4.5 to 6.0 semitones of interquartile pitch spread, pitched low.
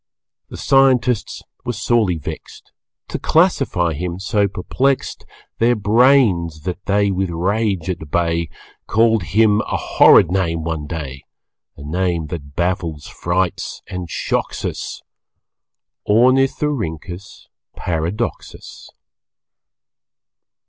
Yes: average, 5.0 semitones; very low, 95 Hz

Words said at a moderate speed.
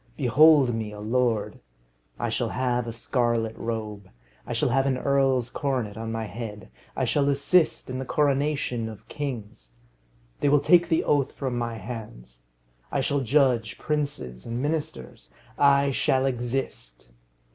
Yes: average, 150 wpm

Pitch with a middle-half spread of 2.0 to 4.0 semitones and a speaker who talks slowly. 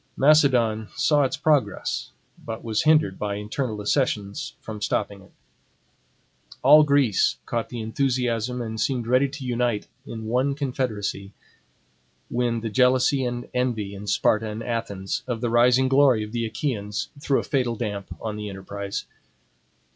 No: average, 3.6 semitones; average, 145 wpm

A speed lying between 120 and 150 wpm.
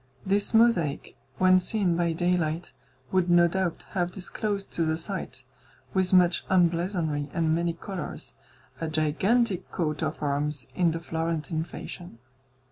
Yes: slow, 135 wpm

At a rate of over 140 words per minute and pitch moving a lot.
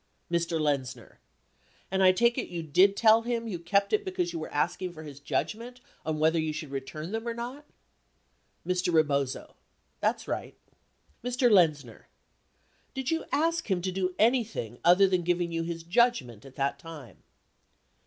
Yes: average, 165 wpm; wide, 6.0 semitones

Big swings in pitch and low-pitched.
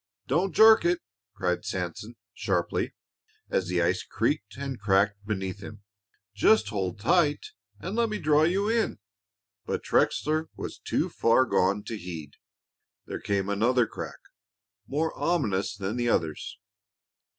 Yes: wide, 8.0 semitones; low, 110 Hz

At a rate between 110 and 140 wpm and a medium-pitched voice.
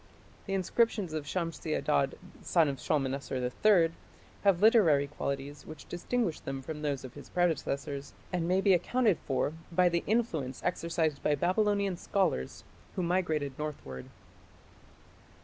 Yes: slow, 135 wpm; medium, 165 Hz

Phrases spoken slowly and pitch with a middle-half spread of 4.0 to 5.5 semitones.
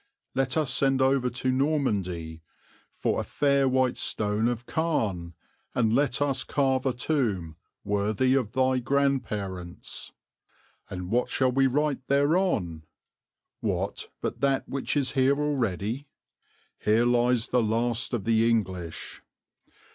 Yes: slow, 130 wpm; average, 4.3 semitones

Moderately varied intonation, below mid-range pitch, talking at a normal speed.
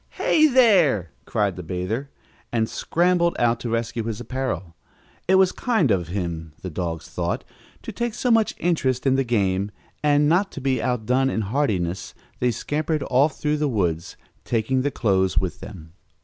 No: wide, 7.9 semitones; low, 120 Hz; average, 170 wpm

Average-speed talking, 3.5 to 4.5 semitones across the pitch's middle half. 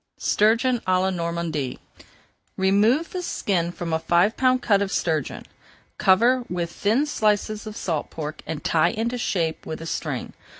No: average, 160 wpm; average, 5.0 semitones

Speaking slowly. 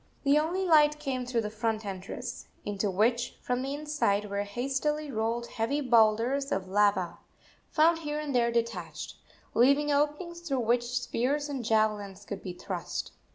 No: average, 155 wpm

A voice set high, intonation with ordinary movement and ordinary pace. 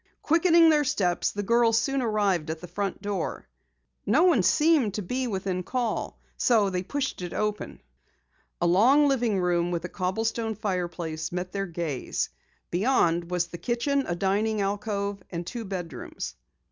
Yes: high, 200 Hz; average, 5.0 semitones; average, 160 wpm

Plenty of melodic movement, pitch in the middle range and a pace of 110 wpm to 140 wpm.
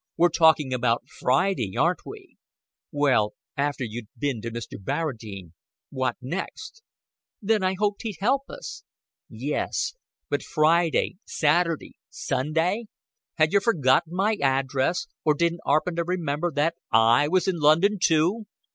Yes: wide, 5.9 semitones; medium, 160 Hz; slow, 135 wpm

